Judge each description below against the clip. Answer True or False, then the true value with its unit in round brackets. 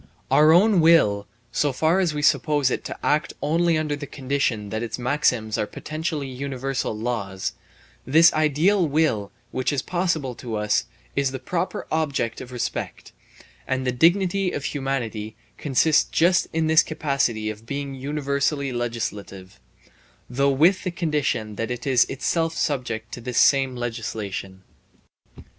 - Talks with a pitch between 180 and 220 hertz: False (135 Hz)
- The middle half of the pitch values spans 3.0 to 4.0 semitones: False (4.8 semitones)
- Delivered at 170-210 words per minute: False (150 wpm)